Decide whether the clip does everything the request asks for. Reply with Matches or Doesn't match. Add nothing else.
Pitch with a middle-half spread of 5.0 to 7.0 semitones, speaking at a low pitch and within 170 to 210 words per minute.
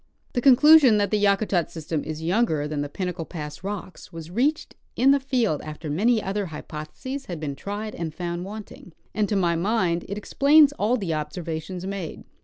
Doesn't match